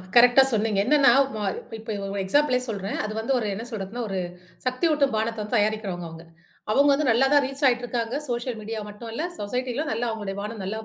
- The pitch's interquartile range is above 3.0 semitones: Yes, average, 3.4 semitones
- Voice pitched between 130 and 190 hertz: No, high, 225 Hz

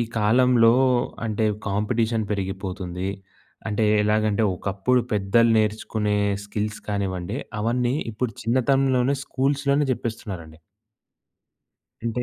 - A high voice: No, low, 110 Hz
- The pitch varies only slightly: No, average, 3.2 semitones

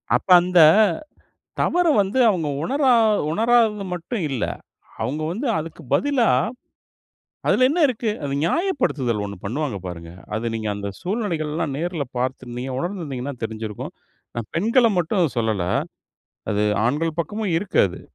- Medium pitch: Yes, medium, 165 Hz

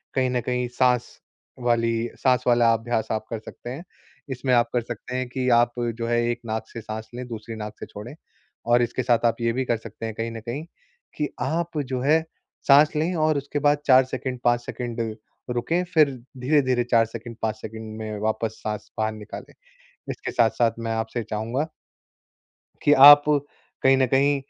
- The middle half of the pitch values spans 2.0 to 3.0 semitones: Yes, average, 2.7 semitones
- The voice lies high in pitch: No, low, 120 Hz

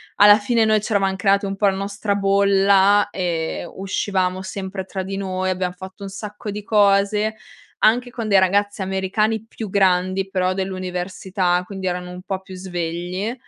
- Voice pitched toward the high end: Yes, high, 195 Hz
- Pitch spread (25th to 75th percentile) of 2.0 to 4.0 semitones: No, narrow, 1.6 semitones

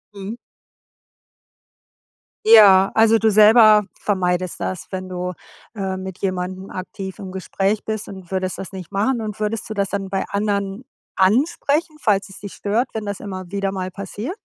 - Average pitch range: No, narrow, 2.3 semitones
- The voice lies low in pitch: No, high, 200 Hz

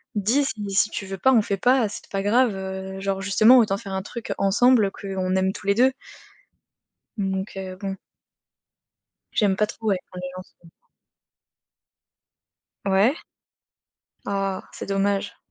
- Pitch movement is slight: Yes, narrow, 2.1 semitones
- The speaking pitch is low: No, high, 195 Hz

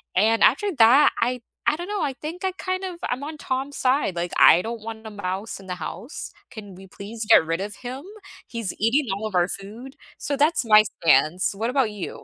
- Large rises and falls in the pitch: Yes, wide, 5.9 semitones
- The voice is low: No, high, 225 Hz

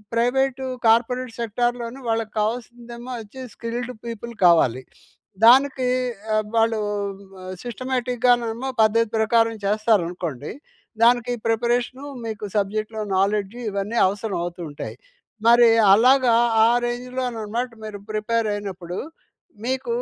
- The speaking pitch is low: No, high, 230 Hz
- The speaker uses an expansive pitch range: No, narrow, 2.5 semitones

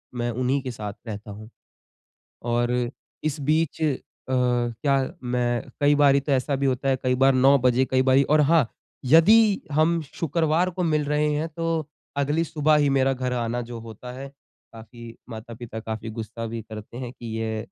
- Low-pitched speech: Yes, low, 130 Hz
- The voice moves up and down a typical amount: Yes, average, 3.9 semitones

